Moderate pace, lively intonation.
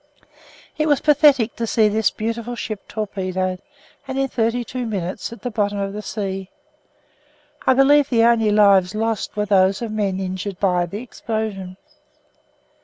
No: average, 160 wpm; average, 3.3 semitones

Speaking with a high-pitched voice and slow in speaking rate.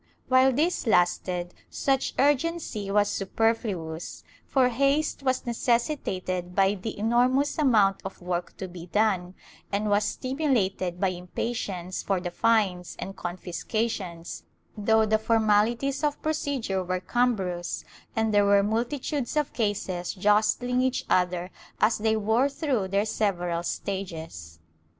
Yes: high, 210 Hz; slow, 130 wpm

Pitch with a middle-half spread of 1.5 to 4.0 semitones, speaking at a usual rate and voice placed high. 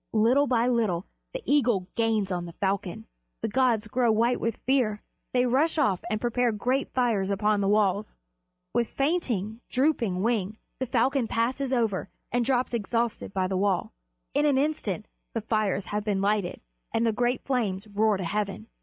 Yes: average, 3.6 semitones; average, 170 wpm; high, 225 Hz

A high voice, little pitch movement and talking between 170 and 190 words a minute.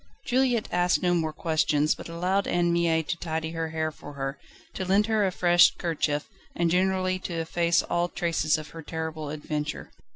No: medium, 170 Hz; narrow, 2.1 semitones; average, 185 wpm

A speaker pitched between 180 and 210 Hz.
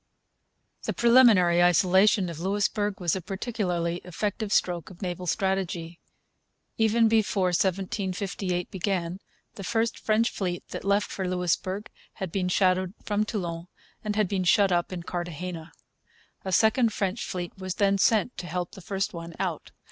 Yes: high, 190 Hz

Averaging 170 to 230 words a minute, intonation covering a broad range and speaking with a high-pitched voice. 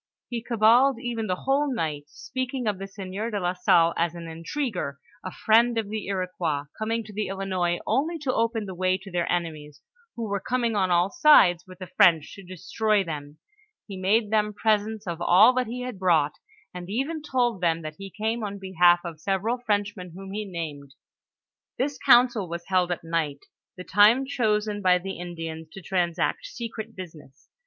No: average, 190 wpm; average, 4.5 semitones; high, 195 Hz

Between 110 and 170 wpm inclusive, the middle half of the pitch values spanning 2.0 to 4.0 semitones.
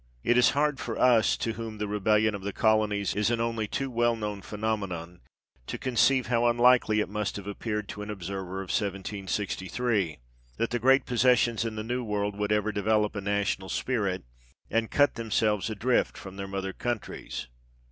No: average, 180 wpm; average, 2.7 semitones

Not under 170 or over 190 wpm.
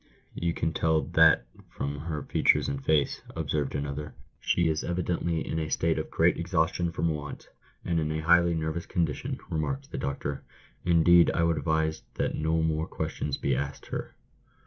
Yes: average, 175 wpm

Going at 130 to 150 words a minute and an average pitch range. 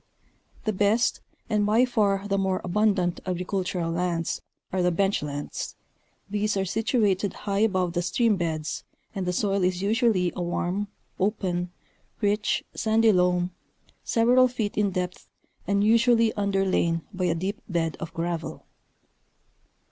Yes: average, 140 wpm; average, 3.0 semitones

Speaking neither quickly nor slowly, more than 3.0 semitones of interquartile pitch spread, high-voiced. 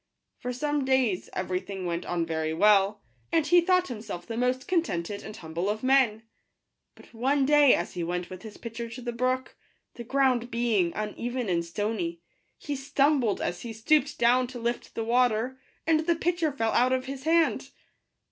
Yes: average, 185 wpm; average, 4.6 semitones; high, 240 Hz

